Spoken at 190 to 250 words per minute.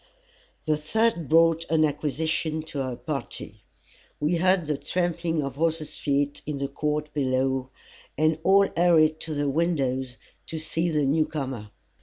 No: average, 150 wpm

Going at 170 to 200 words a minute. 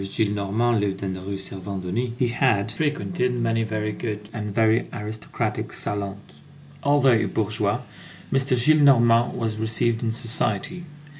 No: slow, 135 wpm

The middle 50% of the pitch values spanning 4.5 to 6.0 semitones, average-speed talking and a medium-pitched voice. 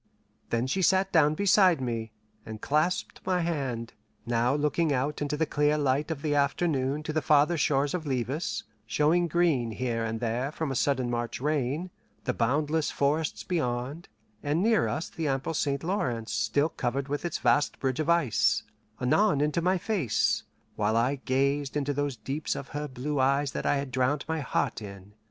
No: average, 3.7 semitones; average, 180 wpm; medium, 145 Hz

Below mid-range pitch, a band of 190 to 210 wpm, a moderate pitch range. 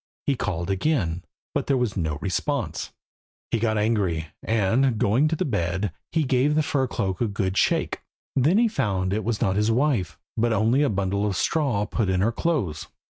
No: low, 110 Hz; average, 195 wpm; wide, 5.8 semitones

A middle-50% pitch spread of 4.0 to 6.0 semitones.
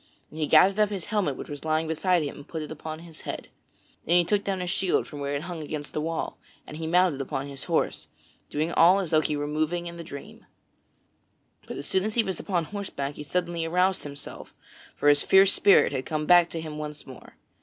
No: average, 3.4 semitones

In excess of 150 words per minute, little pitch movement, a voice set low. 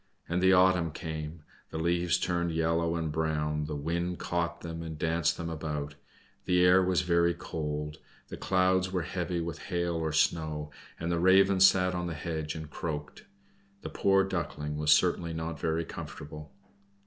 Yes: average, 170 wpm; narrow, 2.1 semitones; very low, 85 Hz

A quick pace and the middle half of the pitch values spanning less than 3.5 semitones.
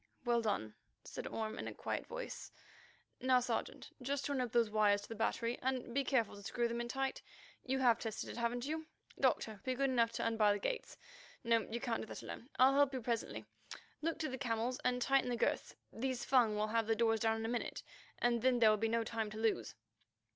Yes: fast, 225 wpm; narrow, 2.6 semitones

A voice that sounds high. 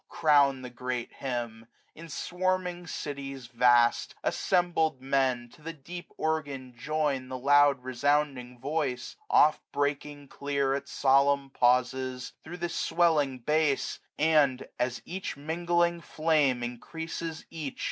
No: medium, 140 Hz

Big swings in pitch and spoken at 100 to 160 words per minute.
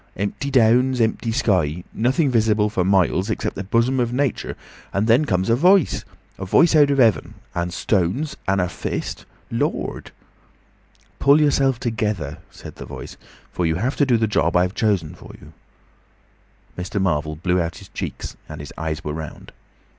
No: wide, 6.0 semitones; average, 170 wpm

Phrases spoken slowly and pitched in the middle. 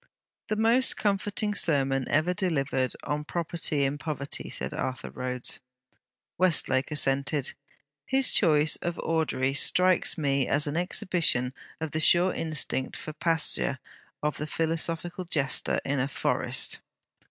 Yes: slow, 130 wpm; medium, 155 Hz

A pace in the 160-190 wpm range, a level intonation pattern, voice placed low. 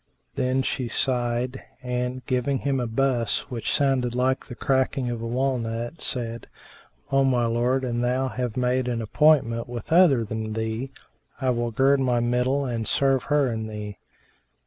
Yes: average, 170 wpm; narrow, 2.1 semitones; low, 125 Hz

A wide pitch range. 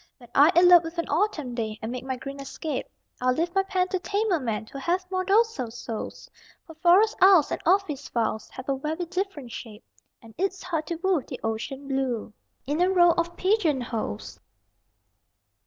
Yes: wide, 6.4 semitones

